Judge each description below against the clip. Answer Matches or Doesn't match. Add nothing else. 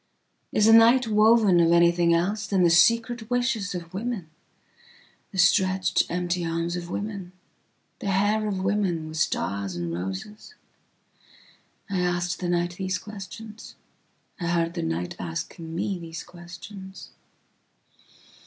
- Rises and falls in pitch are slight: Doesn't match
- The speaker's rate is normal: Doesn't match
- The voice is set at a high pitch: Doesn't match